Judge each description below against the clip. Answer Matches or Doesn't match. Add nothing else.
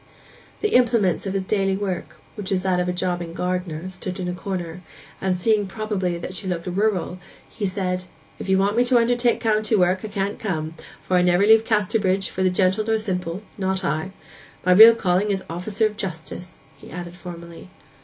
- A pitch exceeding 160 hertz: Matches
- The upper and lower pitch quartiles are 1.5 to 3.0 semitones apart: Matches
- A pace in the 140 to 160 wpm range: Doesn't match